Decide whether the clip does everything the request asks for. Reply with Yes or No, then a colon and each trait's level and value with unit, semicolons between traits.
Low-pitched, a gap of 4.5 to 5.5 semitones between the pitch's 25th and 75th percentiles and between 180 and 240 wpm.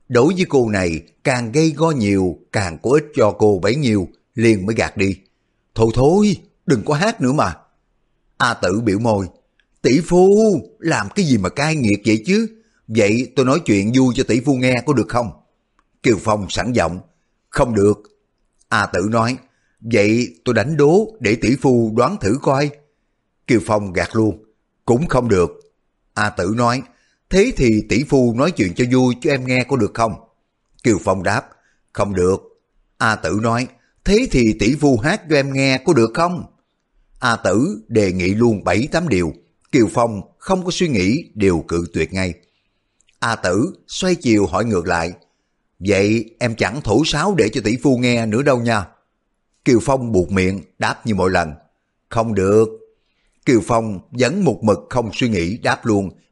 Yes: low, 115 Hz; average, 5.1 semitones; average, 185 wpm